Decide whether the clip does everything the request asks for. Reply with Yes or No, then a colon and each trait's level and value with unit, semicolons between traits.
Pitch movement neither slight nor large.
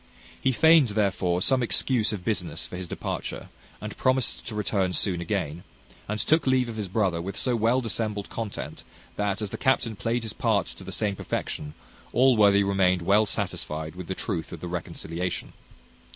Yes: average, 4.2 semitones